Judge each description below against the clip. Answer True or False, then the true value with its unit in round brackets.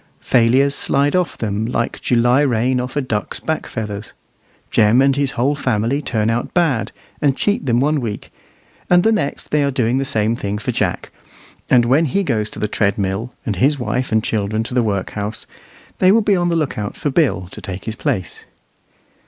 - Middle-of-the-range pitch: False (125 Hz)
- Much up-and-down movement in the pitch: False (4.7 semitones)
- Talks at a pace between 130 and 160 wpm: False (195 wpm)